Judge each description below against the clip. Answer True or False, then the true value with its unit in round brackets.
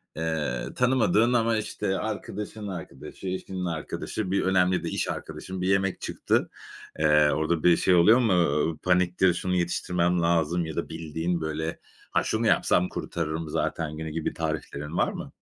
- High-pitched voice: False (90 Hz)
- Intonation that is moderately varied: True (3.1 semitones)